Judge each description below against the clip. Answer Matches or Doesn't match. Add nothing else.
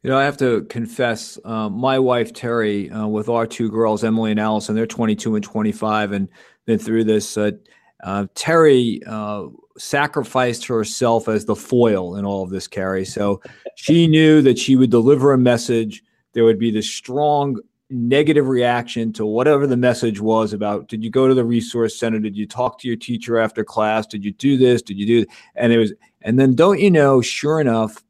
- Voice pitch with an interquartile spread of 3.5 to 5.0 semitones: Doesn't match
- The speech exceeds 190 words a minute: Matches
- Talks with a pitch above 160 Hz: Doesn't match